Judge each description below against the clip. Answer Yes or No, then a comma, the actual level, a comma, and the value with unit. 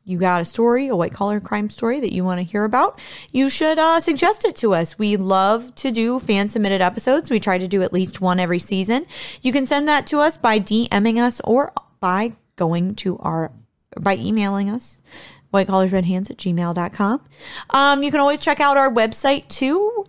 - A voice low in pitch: No, high, 220 Hz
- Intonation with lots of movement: Yes, wide, 6.2 semitones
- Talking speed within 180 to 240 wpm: Yes, average, 200 wpm